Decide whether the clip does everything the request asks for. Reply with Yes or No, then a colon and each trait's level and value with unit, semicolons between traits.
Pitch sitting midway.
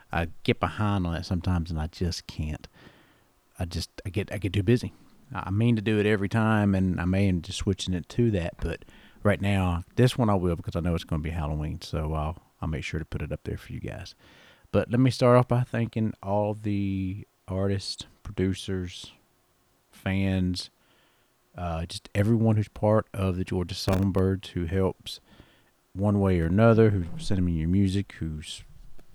No: very low, 95 Hz